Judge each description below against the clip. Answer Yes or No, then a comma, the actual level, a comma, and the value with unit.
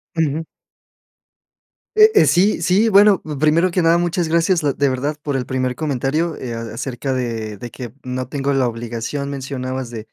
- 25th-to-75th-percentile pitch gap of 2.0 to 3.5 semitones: No, average, 4.8 semitones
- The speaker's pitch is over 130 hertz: Yes, medium, 140 Hz